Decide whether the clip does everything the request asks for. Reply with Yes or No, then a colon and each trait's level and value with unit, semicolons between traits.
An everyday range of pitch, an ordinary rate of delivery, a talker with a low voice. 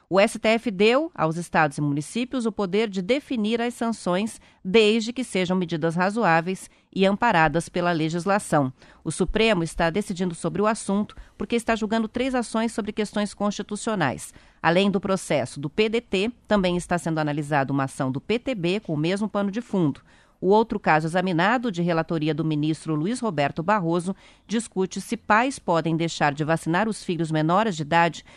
No: average, 5.0 semitones; average, 165 wpm; high, 190 Hz